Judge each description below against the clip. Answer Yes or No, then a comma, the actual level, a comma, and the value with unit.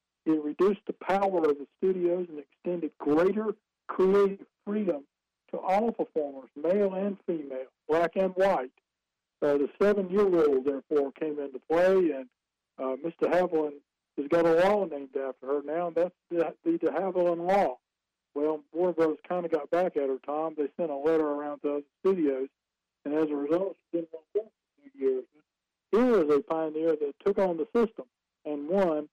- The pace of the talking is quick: No, average, 175 wpm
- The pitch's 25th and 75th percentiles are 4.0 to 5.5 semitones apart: Yes, average, 4.5 semitones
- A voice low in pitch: No, medium, 160 Hz